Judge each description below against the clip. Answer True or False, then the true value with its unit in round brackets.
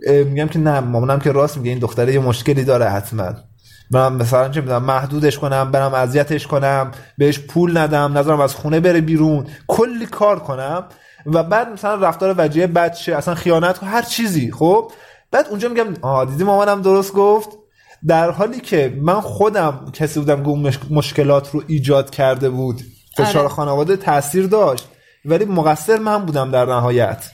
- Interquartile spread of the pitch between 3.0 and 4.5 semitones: False (4.9 semitones)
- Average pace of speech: False (170 wpm)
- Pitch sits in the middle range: True (150 Hz)